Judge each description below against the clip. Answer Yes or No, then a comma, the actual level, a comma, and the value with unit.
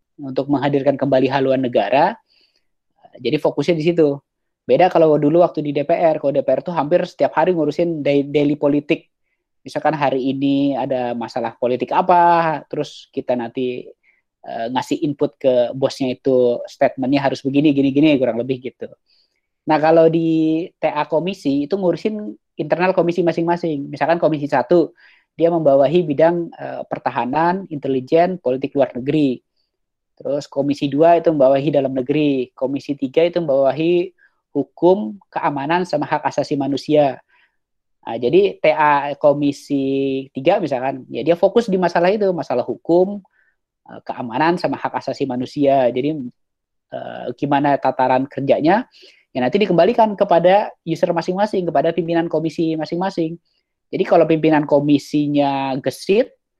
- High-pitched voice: No, medium, 150 Hz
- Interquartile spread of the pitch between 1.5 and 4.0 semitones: Yes, average, 3.7 semitones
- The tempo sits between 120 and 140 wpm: Yes, average, 135 wpm